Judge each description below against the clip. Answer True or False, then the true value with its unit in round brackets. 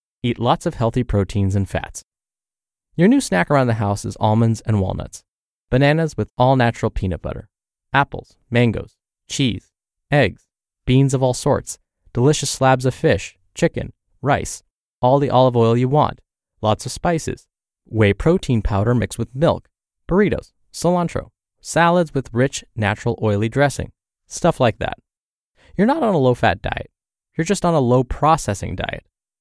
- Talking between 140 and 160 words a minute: True (155 wpm)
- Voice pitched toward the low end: True (120 Hz)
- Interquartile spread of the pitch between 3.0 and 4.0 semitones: False (4.7 semitones)